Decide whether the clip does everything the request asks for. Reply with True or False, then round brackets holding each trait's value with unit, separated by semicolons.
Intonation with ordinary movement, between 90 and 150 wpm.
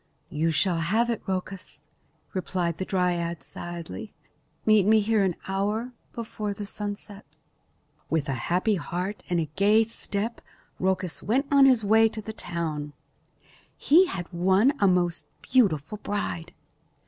True (3.9 semitones; 140 wpm)